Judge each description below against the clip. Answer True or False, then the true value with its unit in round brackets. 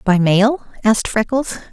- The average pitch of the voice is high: True (220 Hz)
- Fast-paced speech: False (140 wpm)